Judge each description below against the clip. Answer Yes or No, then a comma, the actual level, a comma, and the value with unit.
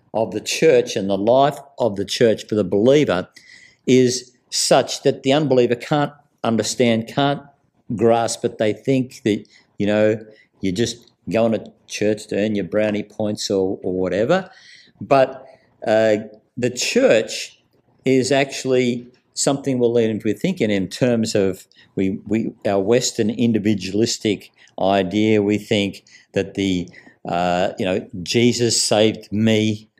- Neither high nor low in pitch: No, low, 110 Hz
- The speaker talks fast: No, average, 140 wpm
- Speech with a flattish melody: No, average, 3.2 semitones